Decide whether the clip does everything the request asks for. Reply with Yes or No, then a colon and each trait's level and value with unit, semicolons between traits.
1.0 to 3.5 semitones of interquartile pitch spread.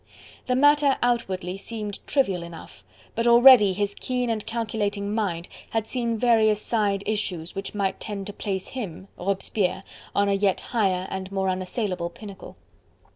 Yes: average, 3.2 semitones